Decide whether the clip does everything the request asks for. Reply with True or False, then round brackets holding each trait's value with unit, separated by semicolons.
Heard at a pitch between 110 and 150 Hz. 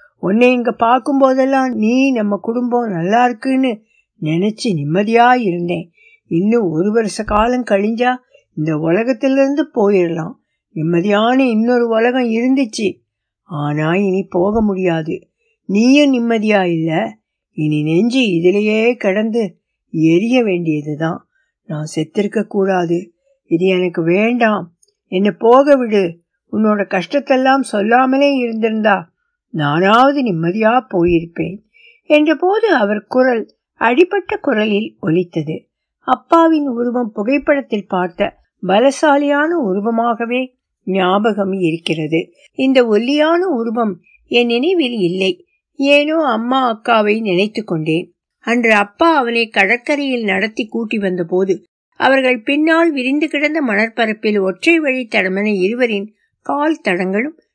False (225 Hz)